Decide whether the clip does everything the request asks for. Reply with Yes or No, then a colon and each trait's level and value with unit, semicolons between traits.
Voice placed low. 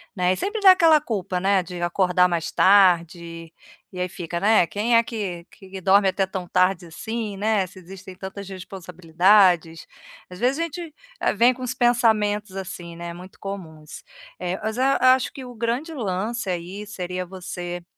No: high, 190 Hz